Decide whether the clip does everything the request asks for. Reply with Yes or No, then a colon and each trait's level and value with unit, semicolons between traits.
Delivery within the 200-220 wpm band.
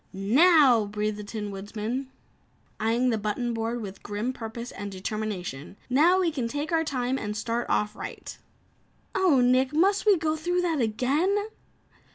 No: average, 165 wpm